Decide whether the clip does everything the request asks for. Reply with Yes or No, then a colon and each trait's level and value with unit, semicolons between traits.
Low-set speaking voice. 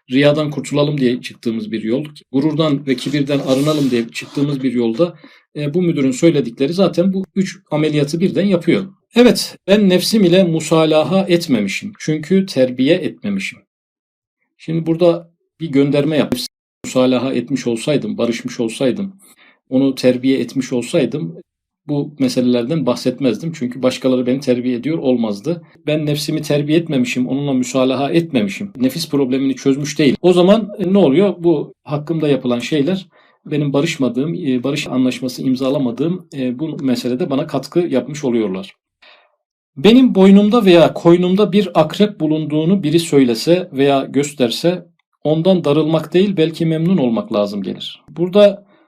No: medium, 150 Hz